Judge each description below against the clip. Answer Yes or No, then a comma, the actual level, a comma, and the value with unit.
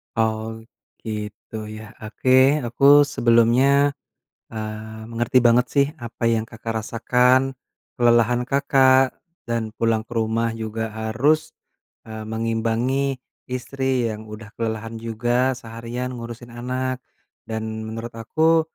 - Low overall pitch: Yes, low, 115 Hz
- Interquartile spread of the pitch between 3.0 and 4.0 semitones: No, narrow, 2.5 semitones